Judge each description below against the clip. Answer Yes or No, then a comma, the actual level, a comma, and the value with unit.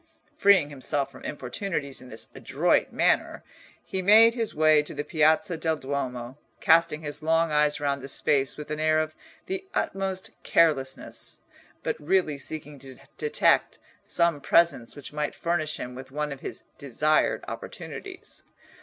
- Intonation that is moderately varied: Yes, average, 3.1 semitones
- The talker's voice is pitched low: No, medium, 150 Hz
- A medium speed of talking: Yes, average, 155 wpm